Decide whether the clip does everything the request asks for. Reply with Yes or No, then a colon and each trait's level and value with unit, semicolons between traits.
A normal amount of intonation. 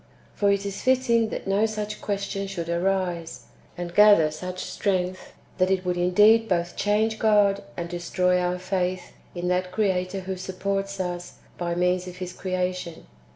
No: narrow, 1.9 semitones